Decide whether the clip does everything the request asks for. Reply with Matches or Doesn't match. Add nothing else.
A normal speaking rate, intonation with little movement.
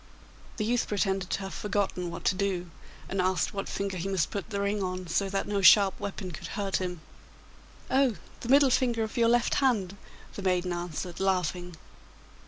Matches